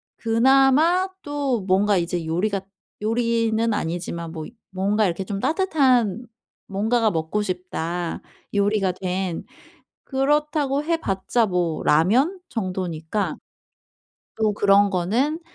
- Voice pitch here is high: Yes, high, 210 Hz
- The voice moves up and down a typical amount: No, wide, 5.8 semitones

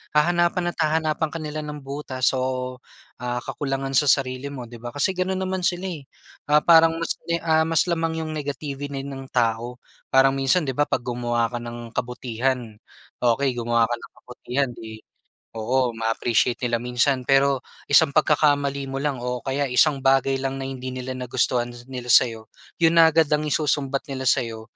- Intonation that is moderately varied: Yes, average, 3.4 semitones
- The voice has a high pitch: No, low, 135 Hz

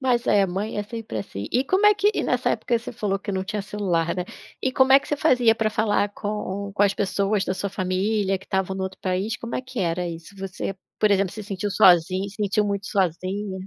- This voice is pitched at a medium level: No, high, 200 Hz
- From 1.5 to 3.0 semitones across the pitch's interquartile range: Yes, narrow, 2.6 semitones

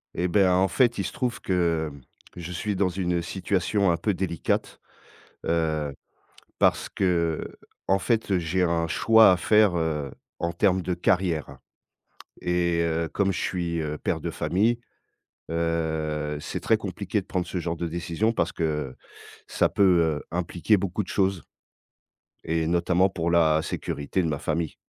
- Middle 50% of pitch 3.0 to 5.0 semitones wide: No, narrow, 2.6 semitones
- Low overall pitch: Yes, very low, 85 Hz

